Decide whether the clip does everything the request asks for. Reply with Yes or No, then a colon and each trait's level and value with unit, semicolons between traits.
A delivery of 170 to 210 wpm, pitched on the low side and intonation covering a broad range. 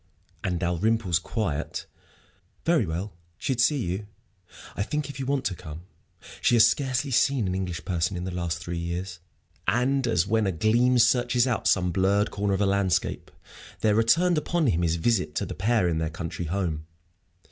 Yes: average, 180 wpm; low, 100 Hz; wide, 5.7 semitones